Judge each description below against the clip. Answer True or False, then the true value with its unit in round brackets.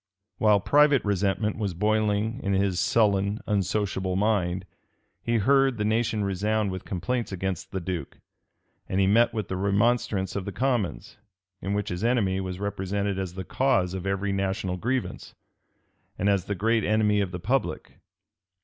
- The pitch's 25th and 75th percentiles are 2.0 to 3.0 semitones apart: True (2.4 semitones)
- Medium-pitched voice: False (100 Hz)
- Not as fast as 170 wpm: True (160 wpm)